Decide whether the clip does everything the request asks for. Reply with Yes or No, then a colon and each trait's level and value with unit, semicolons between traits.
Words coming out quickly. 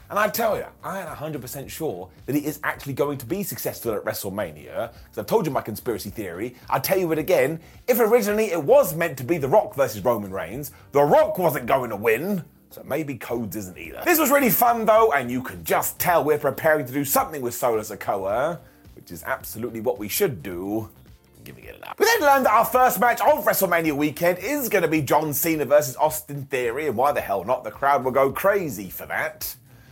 Yes: fast, 230 wpm